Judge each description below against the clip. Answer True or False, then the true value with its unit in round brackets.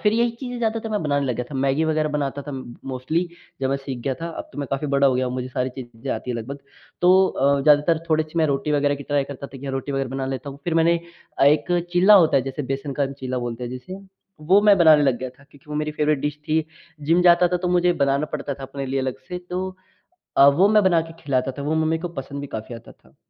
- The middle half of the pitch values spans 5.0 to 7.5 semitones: False (3.7 semitones)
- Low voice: False (145 Hz)